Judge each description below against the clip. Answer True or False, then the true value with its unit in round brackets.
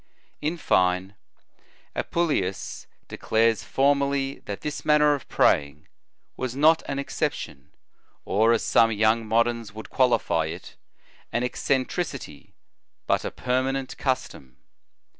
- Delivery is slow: True (110 wpm)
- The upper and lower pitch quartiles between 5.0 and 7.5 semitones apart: True (5.4 semitones)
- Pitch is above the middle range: False (120 Hz)